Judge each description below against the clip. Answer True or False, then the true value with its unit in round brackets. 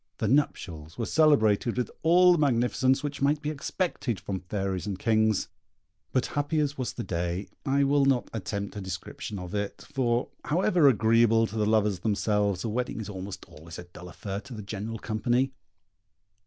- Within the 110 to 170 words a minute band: False (180 wpm)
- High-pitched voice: False (110 Hz)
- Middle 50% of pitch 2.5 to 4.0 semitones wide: False (5.3 semitones)